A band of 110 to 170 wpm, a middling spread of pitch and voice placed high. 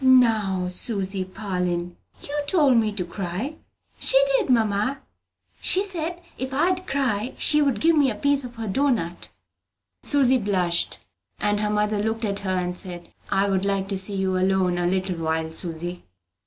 No: average, 165 wpm; wide, 6.0 semitones; high, 205 Hz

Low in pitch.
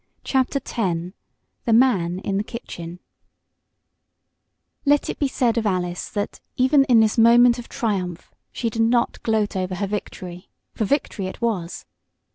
No: high, 220 Hz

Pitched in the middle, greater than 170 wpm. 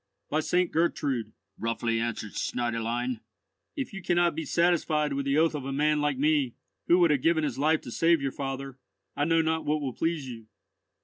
Yes: medium, 145 Hz; average, 200 wpm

